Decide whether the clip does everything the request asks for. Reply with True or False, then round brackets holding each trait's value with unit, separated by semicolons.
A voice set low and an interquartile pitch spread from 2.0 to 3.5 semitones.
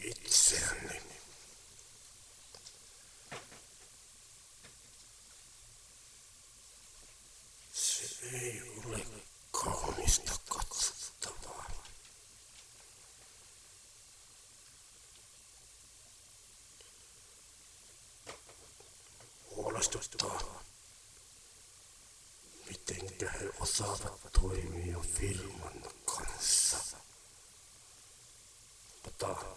True (105 Hz; 3.2 semitones)